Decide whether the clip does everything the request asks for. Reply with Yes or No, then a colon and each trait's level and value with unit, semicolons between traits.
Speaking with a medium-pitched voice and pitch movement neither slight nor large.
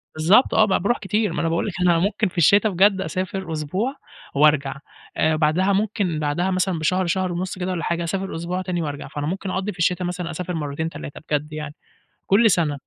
Yes: medium, 180 Hz; average, 3.4 semitones